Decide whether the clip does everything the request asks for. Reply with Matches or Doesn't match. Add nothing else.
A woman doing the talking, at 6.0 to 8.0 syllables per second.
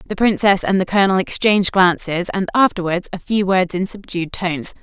Doesn't match